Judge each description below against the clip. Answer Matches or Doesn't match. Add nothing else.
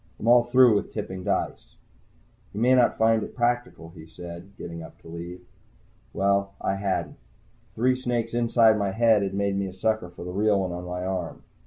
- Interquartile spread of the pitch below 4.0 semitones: Doesn't match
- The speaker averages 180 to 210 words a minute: Matches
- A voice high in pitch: Doesn't match